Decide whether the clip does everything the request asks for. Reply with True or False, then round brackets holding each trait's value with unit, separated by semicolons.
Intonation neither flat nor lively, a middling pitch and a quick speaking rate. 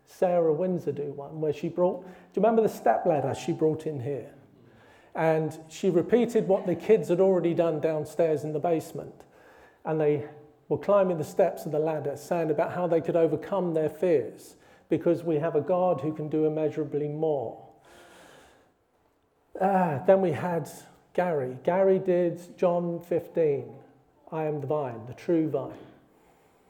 False (3.0 semitones; 165 Hz; 165 wpm)